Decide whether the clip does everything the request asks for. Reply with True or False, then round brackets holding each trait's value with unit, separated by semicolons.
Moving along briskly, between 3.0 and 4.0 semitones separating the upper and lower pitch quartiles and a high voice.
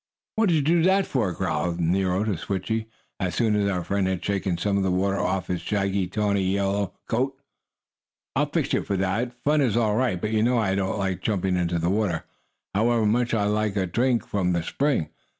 False (215 wpm; 3.4 semitones; 100 Hz)